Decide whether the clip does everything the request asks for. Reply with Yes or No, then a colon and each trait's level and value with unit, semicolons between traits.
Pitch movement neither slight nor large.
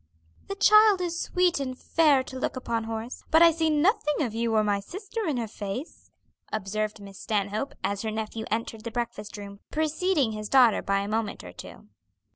No: wide, 6.7 semitones